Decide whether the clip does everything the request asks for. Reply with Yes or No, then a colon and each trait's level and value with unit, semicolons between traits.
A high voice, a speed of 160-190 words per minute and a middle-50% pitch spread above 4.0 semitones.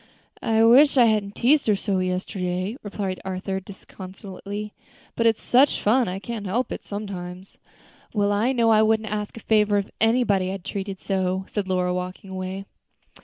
No: high, 200 Hz; average, 170 wpm; average, 2.8 semitones